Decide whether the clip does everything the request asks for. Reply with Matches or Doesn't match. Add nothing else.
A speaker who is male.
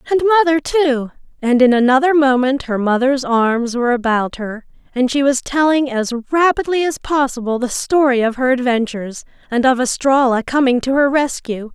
Doesn't match